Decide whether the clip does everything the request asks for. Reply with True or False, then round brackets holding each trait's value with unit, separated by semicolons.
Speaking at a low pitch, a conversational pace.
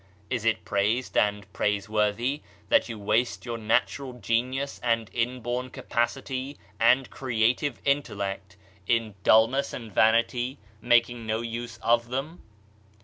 False (120 Hz; 120 wpm)